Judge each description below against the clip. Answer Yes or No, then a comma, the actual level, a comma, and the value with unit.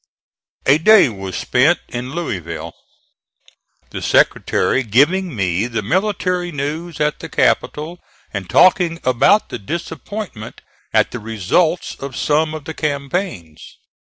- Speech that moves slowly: Yes, slow, 125 wpm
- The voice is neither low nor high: Yes, medium, 145 Hz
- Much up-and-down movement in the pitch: Yes, wide, 7.3 semitones